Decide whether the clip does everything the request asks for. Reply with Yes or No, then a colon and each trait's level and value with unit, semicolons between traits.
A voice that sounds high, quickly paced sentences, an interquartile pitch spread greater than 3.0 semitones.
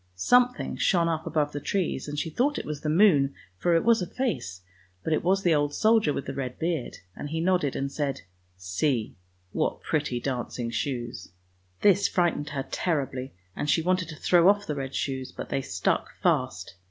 No: medium, 150 Hz; fast, 215 wpm; average, 4.9 semitones